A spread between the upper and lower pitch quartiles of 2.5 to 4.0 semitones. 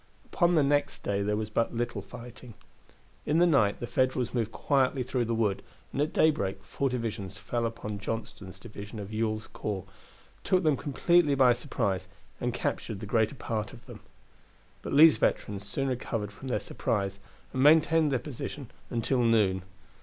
No: average, 4.6 semitones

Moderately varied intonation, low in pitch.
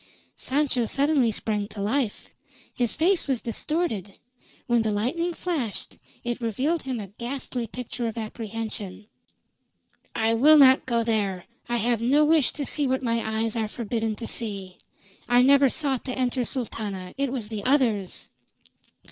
No: average, 3.6 semitones; high, 235 Hz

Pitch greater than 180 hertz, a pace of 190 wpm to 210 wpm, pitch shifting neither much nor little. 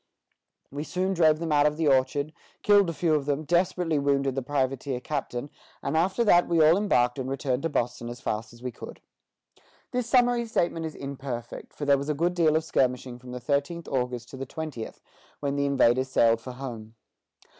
No: medium, 140 Hz; average, 200 wpm; average, 4.3 semitones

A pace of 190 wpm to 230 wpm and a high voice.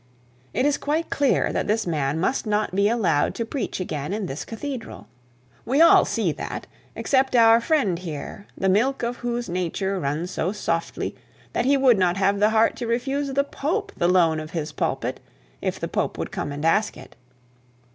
Yes: average, 195 wpm; high, 210 Hz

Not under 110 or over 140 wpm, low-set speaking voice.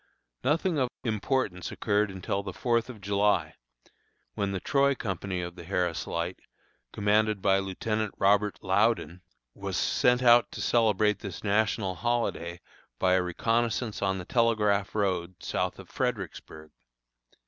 Yes: slow, 135 wpm; low, 100 Hz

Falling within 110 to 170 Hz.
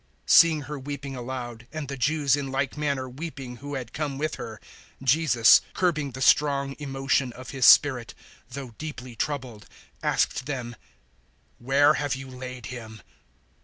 Yes: low, 135 Hz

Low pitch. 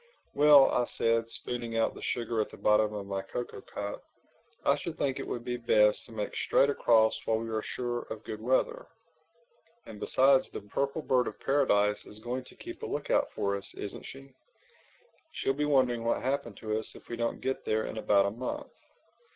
Yes: low, 115 Hz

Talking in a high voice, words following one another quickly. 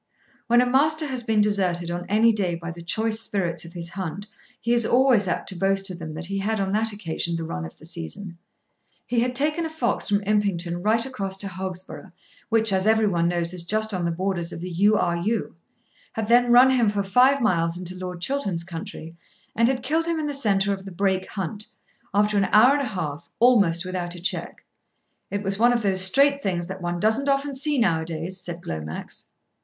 Yes: high, 195 Hz; fast, 225 wpm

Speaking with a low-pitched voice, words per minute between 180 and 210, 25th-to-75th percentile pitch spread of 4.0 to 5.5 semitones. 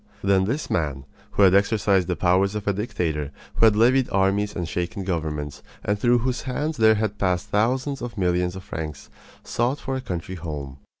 Yes: low, 100 Hz; average, 190 wpm; average, 4.3 semitones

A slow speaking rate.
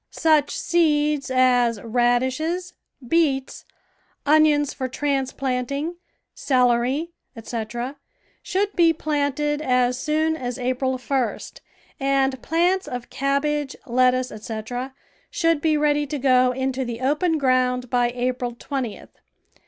Yes: slow, 110 wpm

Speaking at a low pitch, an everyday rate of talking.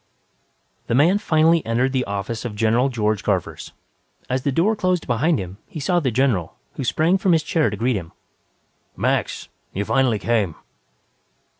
Yes: low, 130 Hz; average, 170 wpm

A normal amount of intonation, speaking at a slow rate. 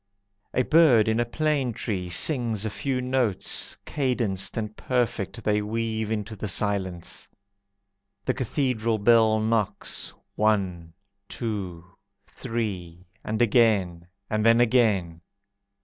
Yes: average, 3.3 semitones; slow, 115 wpm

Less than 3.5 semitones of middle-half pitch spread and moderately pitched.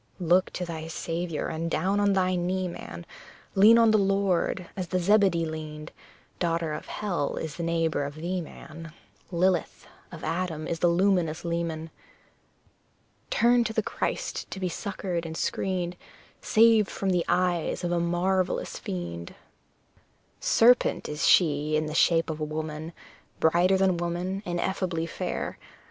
Yes: average, 2.8 semitones; medium, 175 Hz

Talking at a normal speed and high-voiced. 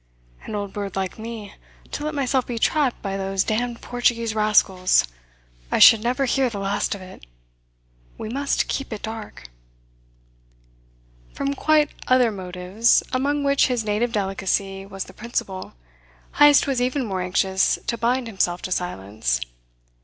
Yes: average, 150 wpm; high, 220 Hz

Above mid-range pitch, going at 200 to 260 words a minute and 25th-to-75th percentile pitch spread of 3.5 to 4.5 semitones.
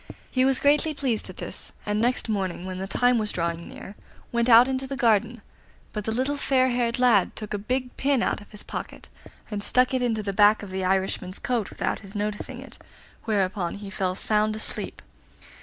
Yes: high, 215 Hz; fast, 205 wpm; average, 4.0 semitones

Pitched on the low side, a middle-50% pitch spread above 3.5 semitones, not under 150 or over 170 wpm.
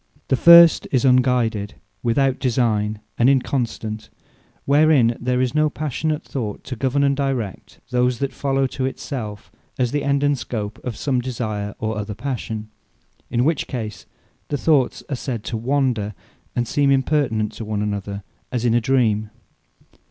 Yes: low, 125 Hz; average, 4.0 semitones; average, 160 wpm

